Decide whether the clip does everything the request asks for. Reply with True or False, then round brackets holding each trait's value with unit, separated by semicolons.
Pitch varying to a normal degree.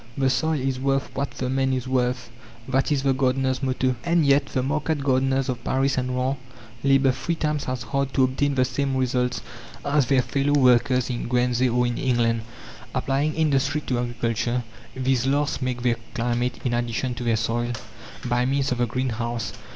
False (1.9 semitones)